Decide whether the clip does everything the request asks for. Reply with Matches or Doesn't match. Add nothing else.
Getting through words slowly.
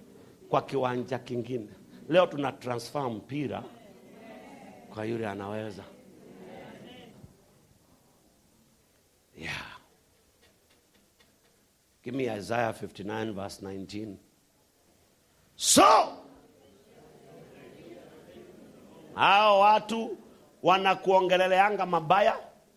Matches